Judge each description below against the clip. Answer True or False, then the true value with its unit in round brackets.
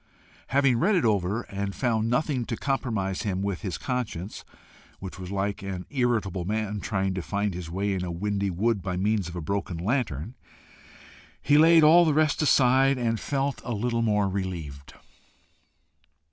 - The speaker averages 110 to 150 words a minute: False (165 wpm)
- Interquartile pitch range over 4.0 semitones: True (4.7 semitones)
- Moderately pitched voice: False (105 Hz)